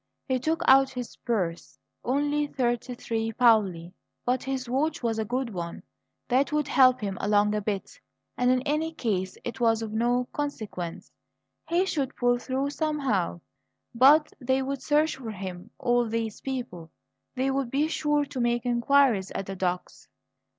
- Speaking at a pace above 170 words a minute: No, average, 165 wpm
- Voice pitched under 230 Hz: No, high, 245 Hz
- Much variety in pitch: No, average, 4.1 semitones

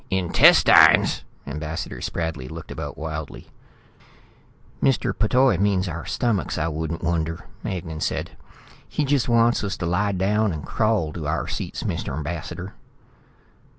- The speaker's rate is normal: No, slow, 130 wpm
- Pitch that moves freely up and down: No, average, 4.6 semitones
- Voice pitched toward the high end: No, very low, 85 Hz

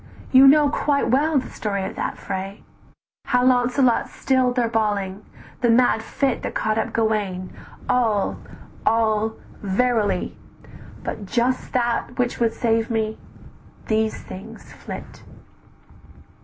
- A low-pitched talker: No, high, 230 Hz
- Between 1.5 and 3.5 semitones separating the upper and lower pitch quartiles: Yes, average, 2.7 semitones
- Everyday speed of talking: No, slow, 125 wpm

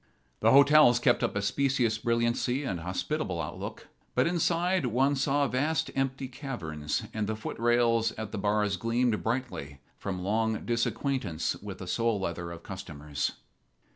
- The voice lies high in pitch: No, low, 115 Hz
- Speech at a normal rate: Yes, average, 145 wpm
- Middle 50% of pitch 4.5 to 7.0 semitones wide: Yes, wide, 5.4 semitones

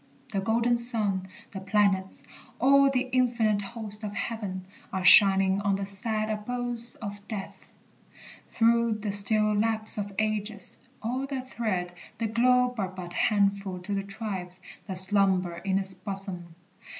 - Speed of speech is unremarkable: Yes, average, 150 wpm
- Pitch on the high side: Yes, high, 205 Hz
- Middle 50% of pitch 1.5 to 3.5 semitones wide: Yes, average, 3.0 semitones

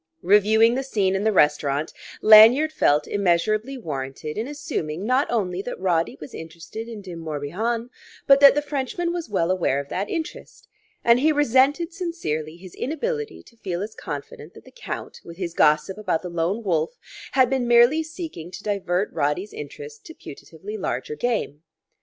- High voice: Yes, high, 210 Hz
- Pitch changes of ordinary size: No, wide, 8.0 semitones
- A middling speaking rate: Yes, average, 170 wpm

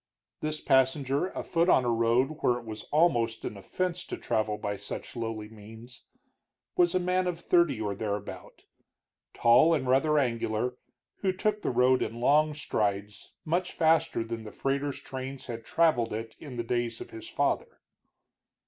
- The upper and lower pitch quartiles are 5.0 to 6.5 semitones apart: Yes, wide, 5.5 semitones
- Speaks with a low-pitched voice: Yes, low, 125 Hz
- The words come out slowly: No, average, 165 wpm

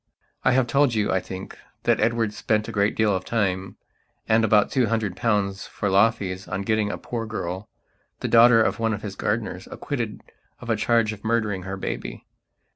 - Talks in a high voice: No, low, 110 Hz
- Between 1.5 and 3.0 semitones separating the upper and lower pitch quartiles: Yes, narrow, 2.5 semitones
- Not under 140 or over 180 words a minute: No, average, 200 wpm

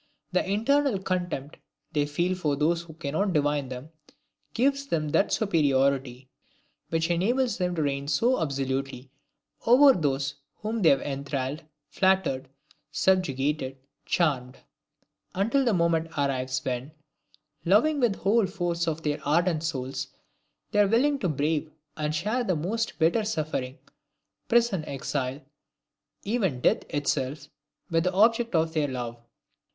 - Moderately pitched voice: Yes, medium, 160 Hz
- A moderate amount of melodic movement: No, wide, 5.8 semitones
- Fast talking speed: No, slow, 135 wpm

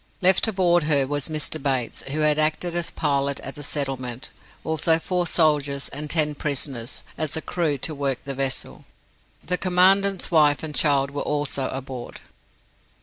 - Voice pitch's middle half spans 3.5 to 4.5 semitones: No, average, 2.7 semitones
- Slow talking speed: No, average, 160 wpm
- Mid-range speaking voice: Yes, medium, 150 Hz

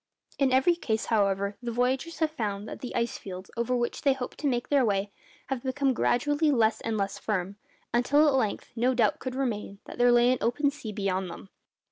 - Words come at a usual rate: No, fast, 210 wpm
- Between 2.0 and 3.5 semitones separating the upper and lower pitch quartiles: No, average, 4.1 semitones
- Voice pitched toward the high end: Yes, high, 240 Hz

